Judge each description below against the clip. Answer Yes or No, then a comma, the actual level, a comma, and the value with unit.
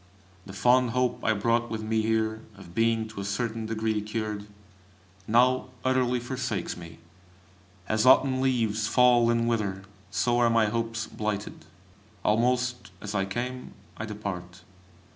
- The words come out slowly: No, average, 145 wpm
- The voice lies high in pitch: No, low, 115 Hz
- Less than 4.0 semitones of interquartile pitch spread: Yes, narrow, 2.4 semitones